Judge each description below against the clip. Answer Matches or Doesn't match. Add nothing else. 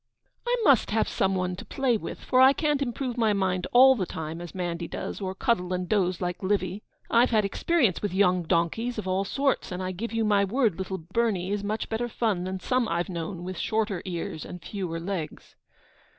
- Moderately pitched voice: Doesn't match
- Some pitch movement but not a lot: Matches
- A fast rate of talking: Matches